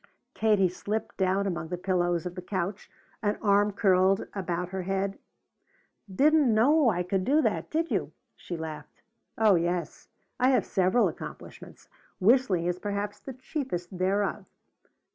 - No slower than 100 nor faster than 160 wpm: Yes, average, 145 wpm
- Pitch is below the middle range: No, high, 195 Hz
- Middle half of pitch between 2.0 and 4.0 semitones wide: Yes, average, 3.3 semitones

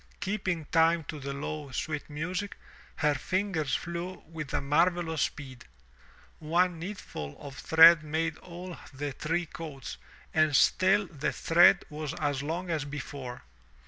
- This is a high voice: No, medium, 160 Hz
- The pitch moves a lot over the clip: No, average, 3.0 semitones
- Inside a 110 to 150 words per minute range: Yes, average, 140 wpm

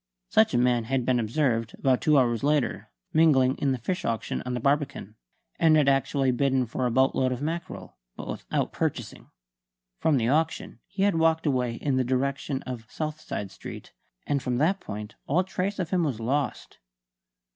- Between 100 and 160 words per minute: No, average, 180 wpm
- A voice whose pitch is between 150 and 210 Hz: No, low, 135 Hz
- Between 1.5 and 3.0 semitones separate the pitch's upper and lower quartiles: No, average, 3.8 semitones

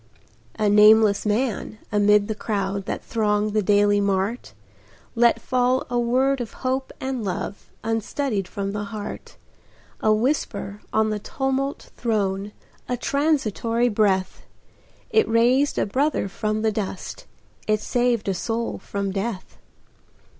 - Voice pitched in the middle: No, high, 215 Hz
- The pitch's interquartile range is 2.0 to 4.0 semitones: Yes, average, 3.3 semitones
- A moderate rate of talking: No, slow, 130 wpm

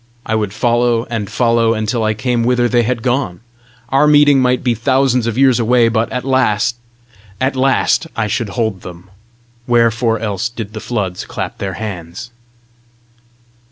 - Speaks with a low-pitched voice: Yes, low, 115 Hz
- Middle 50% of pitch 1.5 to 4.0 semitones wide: Yes, narrow, 2.6 semitones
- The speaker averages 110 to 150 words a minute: No, average, 160 wpm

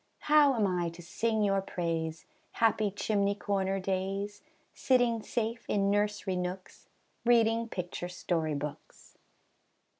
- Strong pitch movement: No, average, 3.6 semitones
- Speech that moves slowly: Yes, slow, 120 wpm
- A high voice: Yes, high, 200 Hz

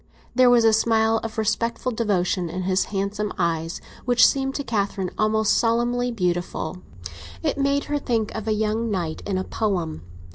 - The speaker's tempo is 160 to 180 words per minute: Yes, average, 170 wpm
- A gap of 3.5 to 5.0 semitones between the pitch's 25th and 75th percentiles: Yes, average, 3.8 semitones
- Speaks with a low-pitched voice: No, high, 220 Hz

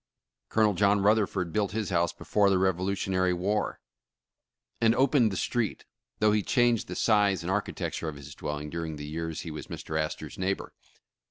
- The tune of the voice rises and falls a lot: No, average, 3.9 semitones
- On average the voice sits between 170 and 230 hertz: No, very low, 95 Hz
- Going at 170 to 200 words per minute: Yes, average, 180 wpm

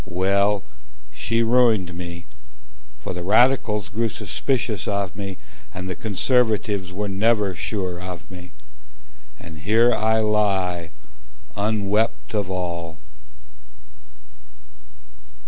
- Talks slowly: Yes, slow, 100 wpm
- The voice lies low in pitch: Yes, low, 100 Hz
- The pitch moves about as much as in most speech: Yes, average, 3.4 semitones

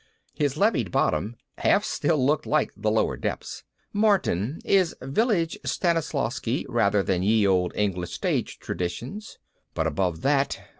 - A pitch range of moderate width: No, wide, 8.4 semitones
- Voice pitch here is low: Yes, low, 125 Hz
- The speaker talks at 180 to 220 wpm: No, slow, 135 wpm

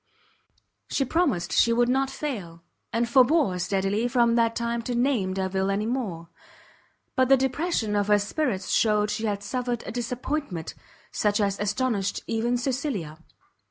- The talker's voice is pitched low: No, high, 230 Hz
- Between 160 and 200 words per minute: No, average, 150 wpm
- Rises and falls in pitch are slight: No, average, 4.2 semitones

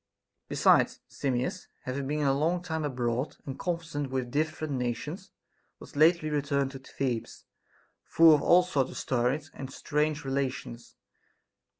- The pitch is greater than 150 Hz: No, medium, 140 Hz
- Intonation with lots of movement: No, average, 3.0 semitones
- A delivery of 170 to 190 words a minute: No, slow, 135 wpm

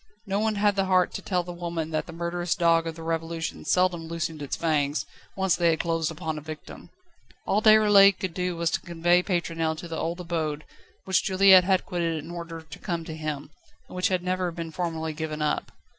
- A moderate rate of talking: No, fast, 220 wpm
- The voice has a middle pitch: Yes, medium, 170 Hz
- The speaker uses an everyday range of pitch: No, narrow, 2.1 semitones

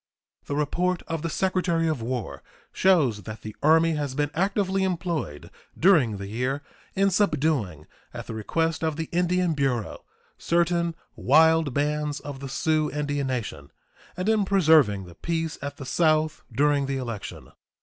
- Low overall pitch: No, medium, 150 Hz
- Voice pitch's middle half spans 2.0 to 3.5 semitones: No, average, 4.4 semitones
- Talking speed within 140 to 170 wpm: Yes, average, 155 wpm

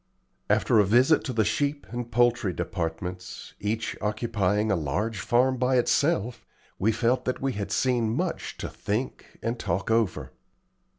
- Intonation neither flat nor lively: Yes, average, 3.4 semitones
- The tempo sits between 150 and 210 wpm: Yes, average, 155 wpm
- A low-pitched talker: Yes, low, 115 Hz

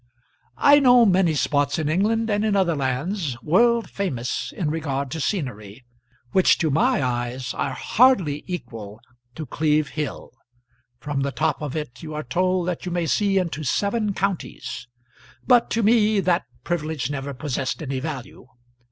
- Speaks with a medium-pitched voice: Yes, medium, 160 Hz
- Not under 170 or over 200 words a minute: No, average, 160 wpm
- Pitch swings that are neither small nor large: No, wide, 6.1 semitones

